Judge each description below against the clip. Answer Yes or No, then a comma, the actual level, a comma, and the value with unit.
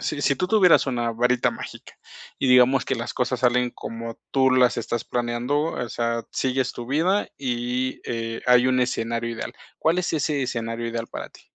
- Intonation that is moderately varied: No, narrow, 2.0 semitones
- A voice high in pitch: No, low, 125 Hz